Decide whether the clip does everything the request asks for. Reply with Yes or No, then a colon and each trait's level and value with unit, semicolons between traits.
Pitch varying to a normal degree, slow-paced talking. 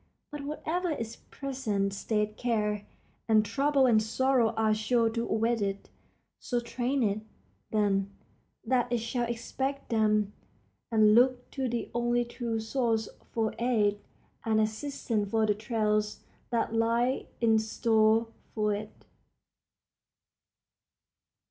No: narrow, 2.2 semitones; slow, 125 wpm